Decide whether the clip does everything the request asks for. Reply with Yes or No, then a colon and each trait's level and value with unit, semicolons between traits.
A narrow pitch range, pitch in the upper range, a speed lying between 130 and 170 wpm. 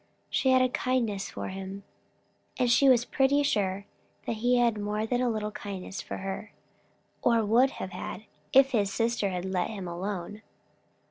No: average, 4.0 semitones; high, 215 Hz; average, 160 wpm